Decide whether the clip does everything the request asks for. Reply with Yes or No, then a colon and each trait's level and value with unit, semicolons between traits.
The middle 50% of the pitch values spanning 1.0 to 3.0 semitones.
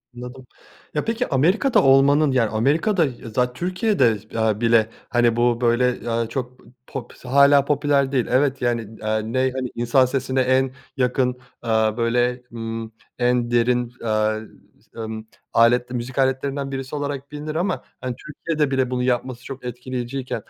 Yes: narrow, 2.4 semitones